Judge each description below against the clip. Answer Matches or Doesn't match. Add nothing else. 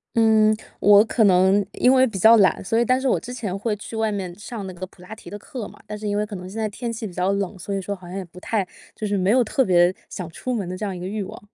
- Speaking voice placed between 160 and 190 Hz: Doesn't match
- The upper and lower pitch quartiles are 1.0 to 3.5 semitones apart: Matches